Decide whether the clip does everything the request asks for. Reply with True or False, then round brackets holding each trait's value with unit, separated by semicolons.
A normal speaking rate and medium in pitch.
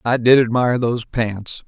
False (180 wpm; 120 Hz)